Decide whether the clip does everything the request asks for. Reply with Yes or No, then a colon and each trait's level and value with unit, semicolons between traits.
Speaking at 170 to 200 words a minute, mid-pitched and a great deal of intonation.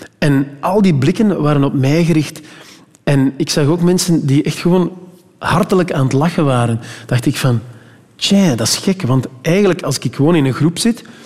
No: average, 195 wpm; medium, 155 Hz; average, 4.7 semitones